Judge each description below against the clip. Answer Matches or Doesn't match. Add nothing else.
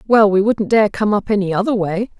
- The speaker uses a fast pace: Matches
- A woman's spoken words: Matches